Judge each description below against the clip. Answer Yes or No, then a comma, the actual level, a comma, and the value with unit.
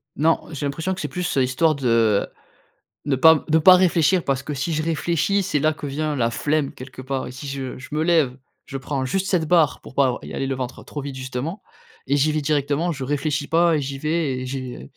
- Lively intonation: No, average, 3.4 semitones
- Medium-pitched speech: Yes, medium, 145 Hz